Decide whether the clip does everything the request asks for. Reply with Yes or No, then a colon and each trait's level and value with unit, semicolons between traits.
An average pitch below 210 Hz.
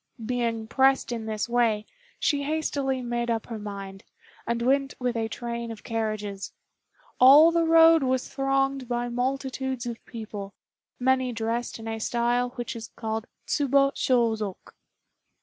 No: high, 240 Hz